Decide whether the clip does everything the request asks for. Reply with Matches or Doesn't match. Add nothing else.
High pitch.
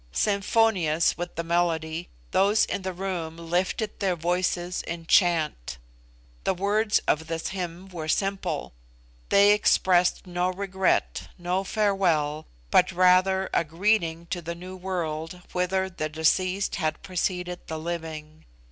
Doesn't match